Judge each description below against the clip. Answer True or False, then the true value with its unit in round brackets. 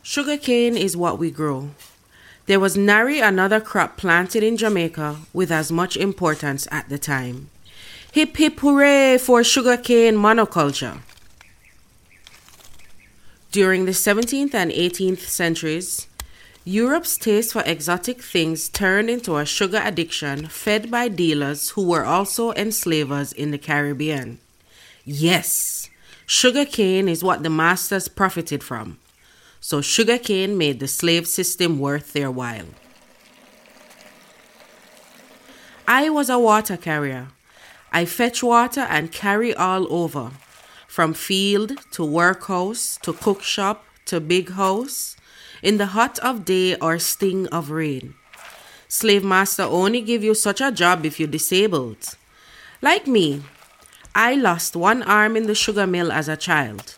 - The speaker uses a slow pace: True (130 wpm)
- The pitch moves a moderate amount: False (6.2 semitones)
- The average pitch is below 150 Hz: False (180 Hz)